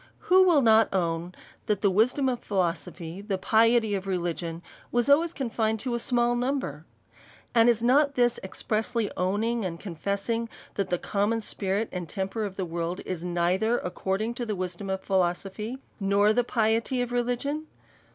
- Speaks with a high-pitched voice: Yes, high, 215 Hz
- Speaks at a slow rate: No, average, 170 wpm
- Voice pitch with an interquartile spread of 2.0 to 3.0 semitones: No, average, 4.3 semitones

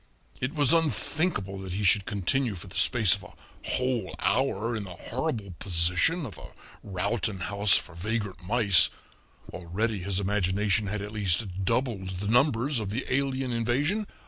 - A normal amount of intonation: Yes, average, 4.5 semitones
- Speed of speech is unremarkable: Yes, average, 160 wpm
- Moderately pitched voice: No, low, 105 Hz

